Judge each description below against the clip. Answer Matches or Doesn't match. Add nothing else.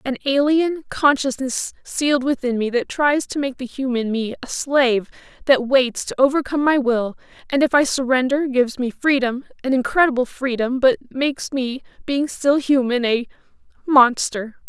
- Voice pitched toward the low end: Doesn't match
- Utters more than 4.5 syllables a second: Matches